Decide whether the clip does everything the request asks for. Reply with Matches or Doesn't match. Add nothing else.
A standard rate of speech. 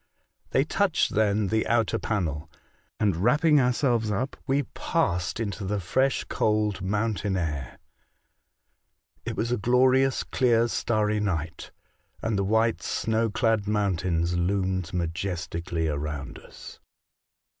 Doesn't match